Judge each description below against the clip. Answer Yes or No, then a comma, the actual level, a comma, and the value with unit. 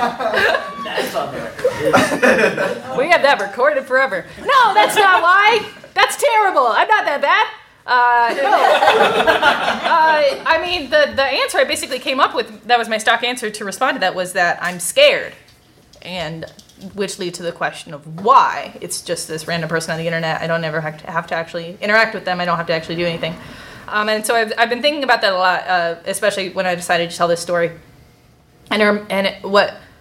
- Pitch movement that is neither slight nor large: No, wide, 8.0 semitones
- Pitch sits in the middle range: No, high, 200 Hz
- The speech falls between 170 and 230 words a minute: Yes, average, 200 wpm